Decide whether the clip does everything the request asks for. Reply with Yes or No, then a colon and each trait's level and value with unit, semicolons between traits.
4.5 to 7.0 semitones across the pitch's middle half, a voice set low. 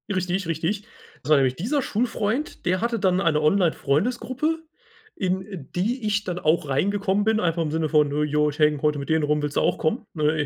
No: wide, 5.4 semitones; medium, 175 Hz